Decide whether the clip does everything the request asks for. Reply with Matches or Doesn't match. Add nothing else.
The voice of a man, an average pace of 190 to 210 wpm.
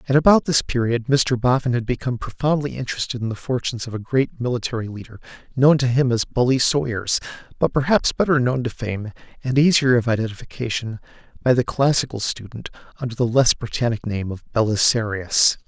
Doesn't match